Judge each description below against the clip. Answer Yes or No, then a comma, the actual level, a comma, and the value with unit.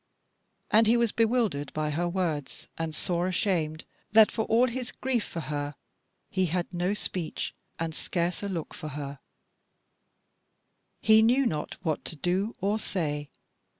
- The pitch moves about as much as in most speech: No, wide, 5.8 semitones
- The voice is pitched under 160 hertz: No, medium, 180 Hz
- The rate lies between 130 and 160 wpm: Yes, average, 150 wpm